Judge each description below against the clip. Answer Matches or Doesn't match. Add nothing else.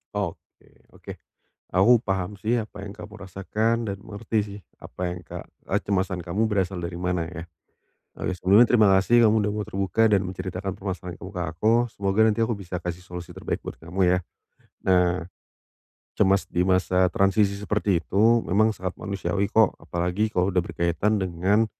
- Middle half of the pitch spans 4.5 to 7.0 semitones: Doesn't match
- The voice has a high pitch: Doesn't match